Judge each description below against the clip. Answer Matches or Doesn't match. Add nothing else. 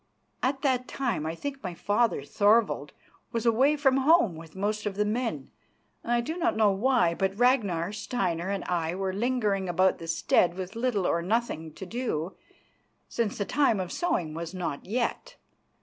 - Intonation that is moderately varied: Doesn't match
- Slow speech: Doesn't match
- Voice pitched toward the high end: Matches